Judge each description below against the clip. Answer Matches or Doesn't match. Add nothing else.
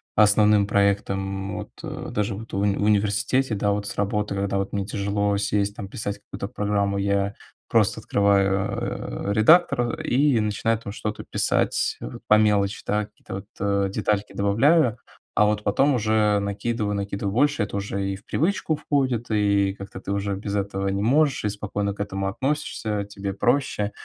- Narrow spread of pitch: Matches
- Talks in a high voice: Doesn't match